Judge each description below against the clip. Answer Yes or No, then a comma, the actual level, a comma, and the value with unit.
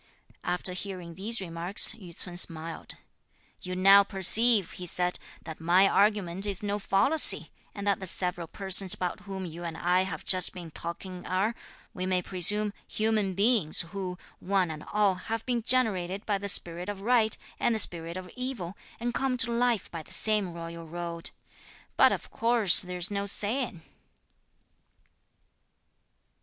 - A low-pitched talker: No, high, 190 Hz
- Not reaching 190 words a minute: Yes, average, 160 wpm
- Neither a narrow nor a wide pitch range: Yes, average, 3.0 semitones